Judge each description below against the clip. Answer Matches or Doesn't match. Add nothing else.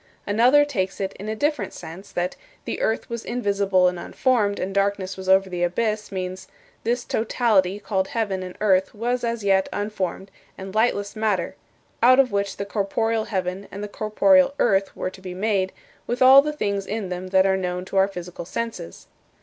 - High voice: Matches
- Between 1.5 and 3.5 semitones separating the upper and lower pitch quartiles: Matches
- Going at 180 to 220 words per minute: Matches